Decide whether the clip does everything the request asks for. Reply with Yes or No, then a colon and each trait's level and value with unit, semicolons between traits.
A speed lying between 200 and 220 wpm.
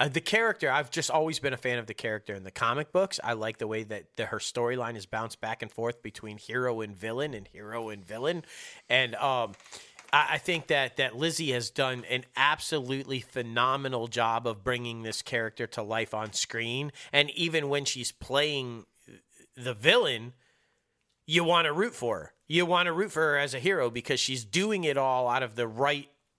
Yes: fast, 205 wpm